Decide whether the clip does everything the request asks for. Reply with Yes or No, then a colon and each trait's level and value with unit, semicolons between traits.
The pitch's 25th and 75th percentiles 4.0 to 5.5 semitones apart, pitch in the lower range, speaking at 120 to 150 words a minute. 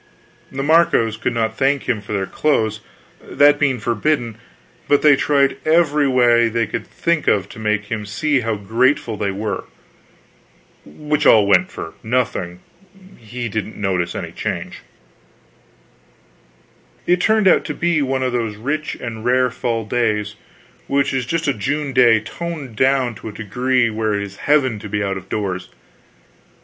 No: average, 4.7 semitones; low, 120 Hz; average, 160 wpm